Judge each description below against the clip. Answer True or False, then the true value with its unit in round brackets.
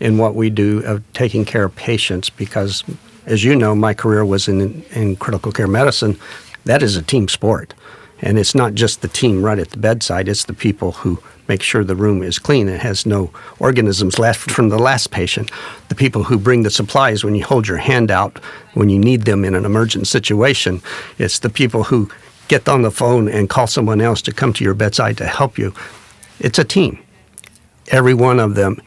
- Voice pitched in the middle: False (110 Hz)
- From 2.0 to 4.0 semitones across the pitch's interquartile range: True (3.2 semitones)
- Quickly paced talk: True (210 wpm)